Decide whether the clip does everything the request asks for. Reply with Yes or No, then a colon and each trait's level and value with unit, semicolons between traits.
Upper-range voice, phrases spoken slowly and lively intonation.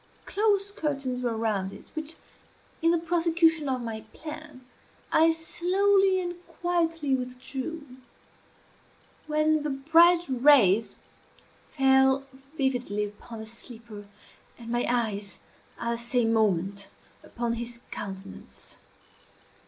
Yes: very high, 265 Hz; slow, 110 wpm; wide, 5.9 semitones